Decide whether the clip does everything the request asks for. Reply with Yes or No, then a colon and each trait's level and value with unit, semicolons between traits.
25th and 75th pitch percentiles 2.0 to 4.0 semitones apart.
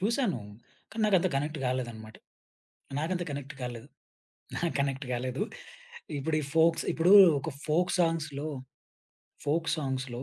No: average, 4.4 semitones